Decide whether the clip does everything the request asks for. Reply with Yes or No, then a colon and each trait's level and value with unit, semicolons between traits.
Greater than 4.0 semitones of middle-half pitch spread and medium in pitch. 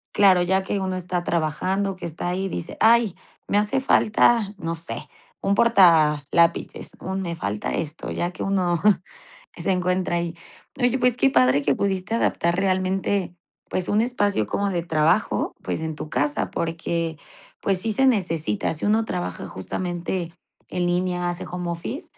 No: average, 3.0 semitones; medium, 180 Hz